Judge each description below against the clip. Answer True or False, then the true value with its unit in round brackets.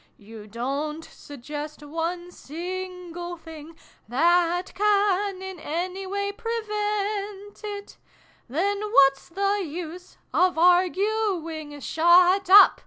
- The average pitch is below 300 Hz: False (355 Hz)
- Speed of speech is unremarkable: False (100 wpm)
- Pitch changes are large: False (4.0 semitones)